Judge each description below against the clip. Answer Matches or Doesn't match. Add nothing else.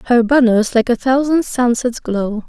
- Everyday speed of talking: Matches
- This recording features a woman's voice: Matches